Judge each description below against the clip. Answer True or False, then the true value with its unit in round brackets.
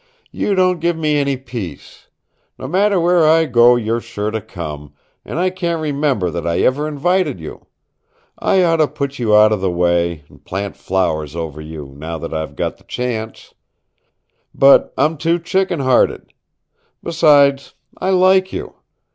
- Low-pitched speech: True (130 Hz)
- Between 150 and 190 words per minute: True (165 wpm)